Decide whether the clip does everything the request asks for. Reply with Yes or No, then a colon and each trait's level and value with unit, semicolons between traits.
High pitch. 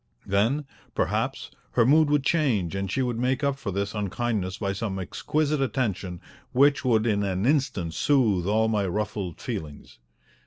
No: low, 110 Hz